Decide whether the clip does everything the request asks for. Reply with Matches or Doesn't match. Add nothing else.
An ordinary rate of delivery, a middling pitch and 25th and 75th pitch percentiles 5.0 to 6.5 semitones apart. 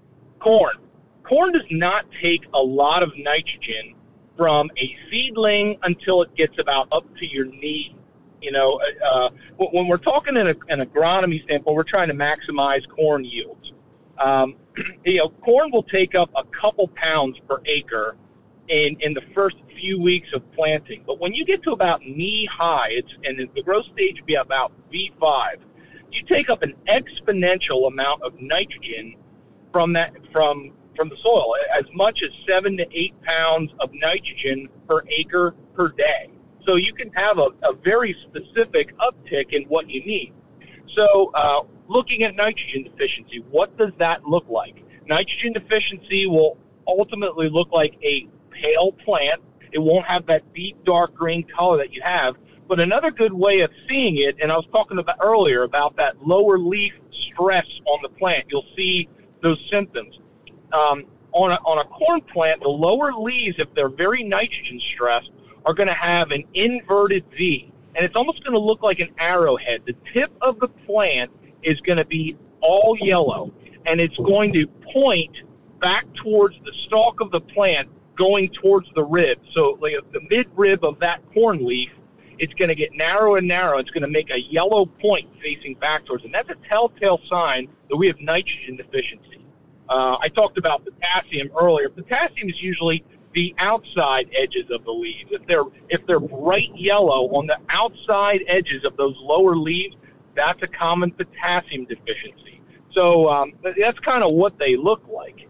Matches